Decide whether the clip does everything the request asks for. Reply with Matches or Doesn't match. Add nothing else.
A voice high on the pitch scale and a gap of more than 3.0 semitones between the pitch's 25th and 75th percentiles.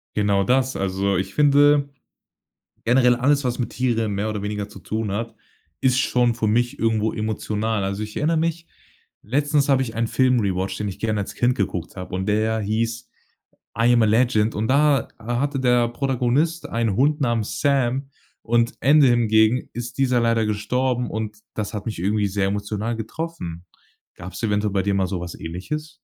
Doesn't match